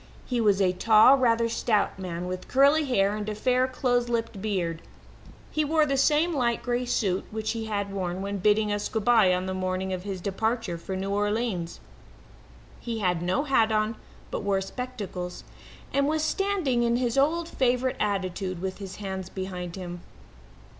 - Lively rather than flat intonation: No, average, 4.7 semitones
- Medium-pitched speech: No, high, 215 Hz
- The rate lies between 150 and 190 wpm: Yes, average, 180 wpm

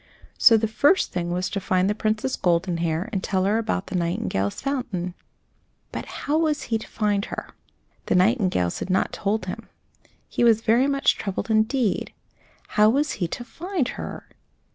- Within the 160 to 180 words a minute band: Yes, average, 170 wpm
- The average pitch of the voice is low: No, high, 215 Hz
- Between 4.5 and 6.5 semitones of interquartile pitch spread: Yes, average, 4.8 semitones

